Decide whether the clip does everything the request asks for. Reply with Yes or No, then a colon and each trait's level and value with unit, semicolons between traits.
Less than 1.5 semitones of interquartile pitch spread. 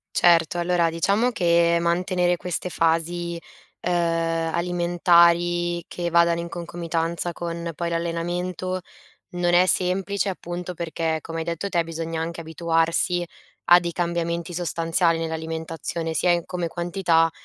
Yes: narrow, 1.0 semitones